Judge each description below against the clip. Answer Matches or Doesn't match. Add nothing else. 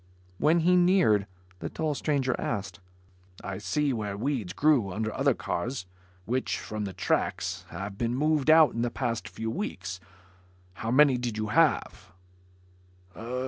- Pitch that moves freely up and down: Matches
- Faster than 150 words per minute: Doesn't match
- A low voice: Matches